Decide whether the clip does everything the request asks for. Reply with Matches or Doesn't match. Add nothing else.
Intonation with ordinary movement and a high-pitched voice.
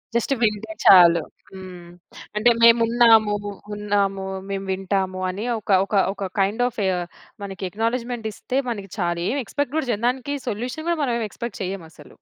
Matches